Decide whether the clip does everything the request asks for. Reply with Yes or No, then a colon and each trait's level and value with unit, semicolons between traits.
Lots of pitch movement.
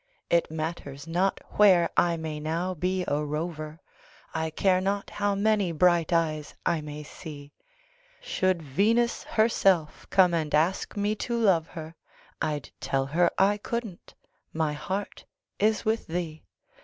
No: average, 4.0 semitones